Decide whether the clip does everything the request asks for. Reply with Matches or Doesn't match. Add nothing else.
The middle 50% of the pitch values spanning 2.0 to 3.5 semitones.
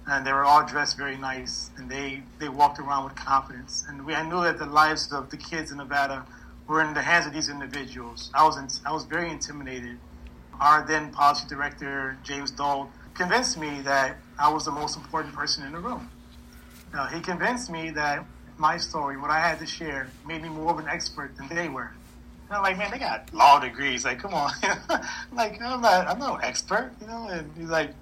Matches